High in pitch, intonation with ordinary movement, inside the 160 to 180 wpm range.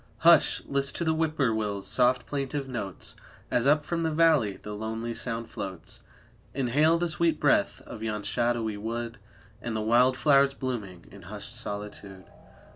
No: low, 120 Hz; average, 4.5 semitones; average, 165 wpm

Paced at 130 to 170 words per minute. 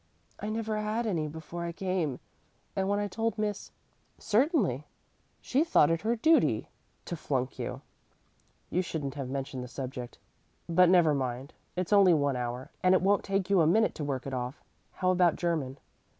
No: average, 180 wpm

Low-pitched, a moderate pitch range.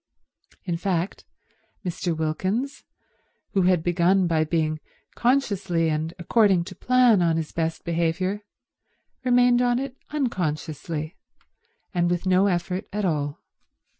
No: medium, 180 Hz; average, 4.0 semitones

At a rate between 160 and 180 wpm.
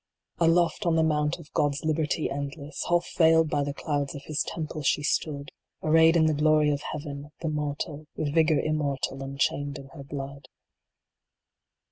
Yes: average, 170 wpm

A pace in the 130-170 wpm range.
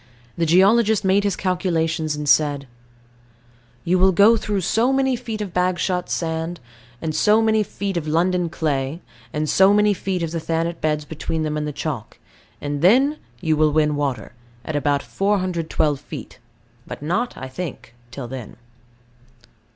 Yes: average, 160 wpm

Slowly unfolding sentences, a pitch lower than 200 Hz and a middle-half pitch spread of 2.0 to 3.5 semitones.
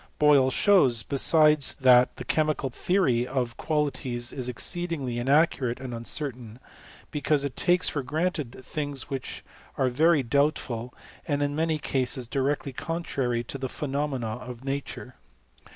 No: average, 150 wpm; low, 135 Hz; average, 3.2 semitones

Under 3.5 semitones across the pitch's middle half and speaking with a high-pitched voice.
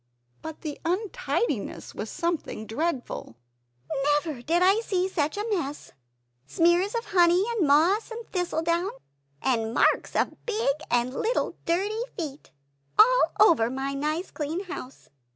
No: wide, 5.5 semitones; very high, 335 Hz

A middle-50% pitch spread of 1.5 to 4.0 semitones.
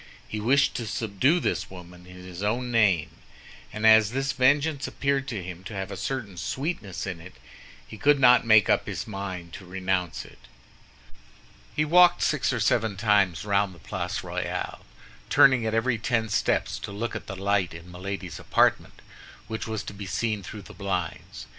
No: average, 4.6 semitones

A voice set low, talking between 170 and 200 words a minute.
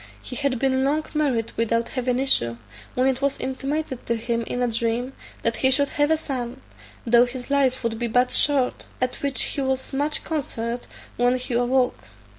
No: very high, 255 Hz; average, 190 wpm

